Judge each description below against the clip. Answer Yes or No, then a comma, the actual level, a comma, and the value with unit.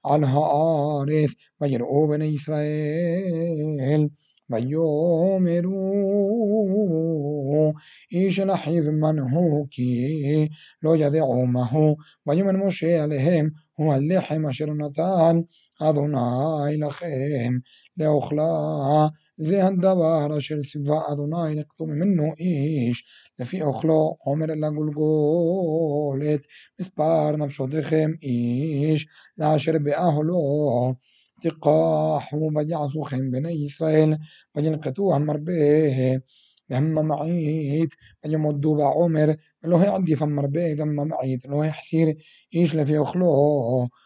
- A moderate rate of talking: No, slow, 90 wpm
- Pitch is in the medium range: Yes, medium, 155 Hz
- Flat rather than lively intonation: Yes, narrow, 1.8 semitones